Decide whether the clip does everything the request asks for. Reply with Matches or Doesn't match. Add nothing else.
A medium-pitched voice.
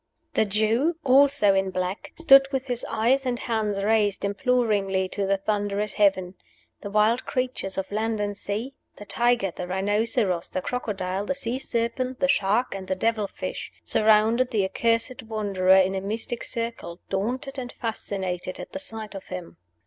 Doesn't match